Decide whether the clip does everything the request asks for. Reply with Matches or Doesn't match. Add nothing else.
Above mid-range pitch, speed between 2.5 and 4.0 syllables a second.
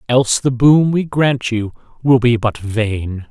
Doesn't match